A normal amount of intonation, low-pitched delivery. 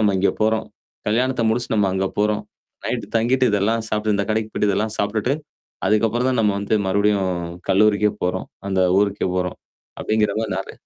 No: narrow, 1.7 semitones; low, 105 Hz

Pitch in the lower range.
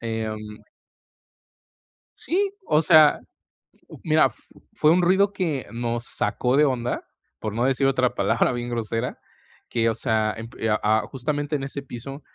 Yes: low, 130 Hz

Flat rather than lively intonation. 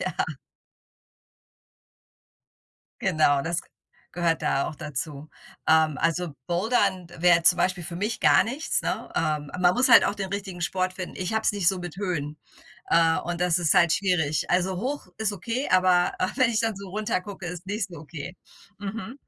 No: average, 3.3 semitones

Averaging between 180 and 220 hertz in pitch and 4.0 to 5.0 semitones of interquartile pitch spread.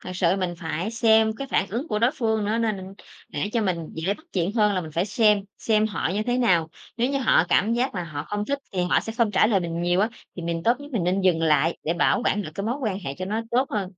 Yes: high, 205 Hz; average, 4.3 semitones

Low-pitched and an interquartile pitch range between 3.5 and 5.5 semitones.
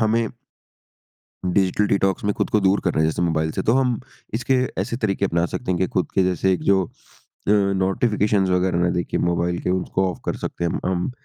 No: very low, 95 Hz; average, 2.8 semitones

